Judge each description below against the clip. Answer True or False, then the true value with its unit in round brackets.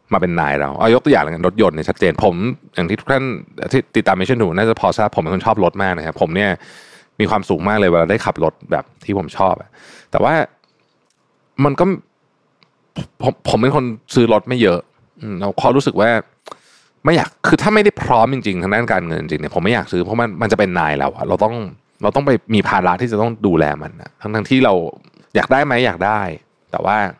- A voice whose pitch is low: True (110 Hz)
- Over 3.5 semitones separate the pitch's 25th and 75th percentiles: True (5.5 semitones)